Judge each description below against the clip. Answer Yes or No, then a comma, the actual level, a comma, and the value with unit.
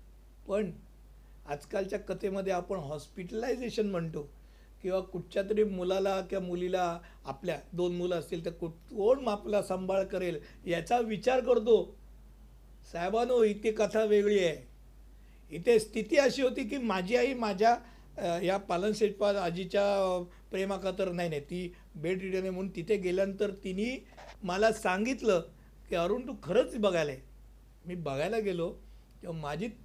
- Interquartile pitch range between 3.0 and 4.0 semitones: Yes, average, 3.3 semitones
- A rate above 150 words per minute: No, average, 135 wpm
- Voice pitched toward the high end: Yes, high, 195 Hz